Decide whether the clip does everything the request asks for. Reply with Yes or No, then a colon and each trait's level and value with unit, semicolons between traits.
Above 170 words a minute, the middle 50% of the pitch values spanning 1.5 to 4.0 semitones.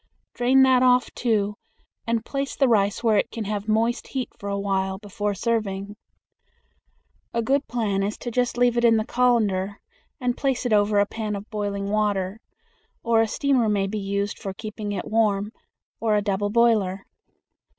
Yes: average, 180 wpm; average, 2.8 semitones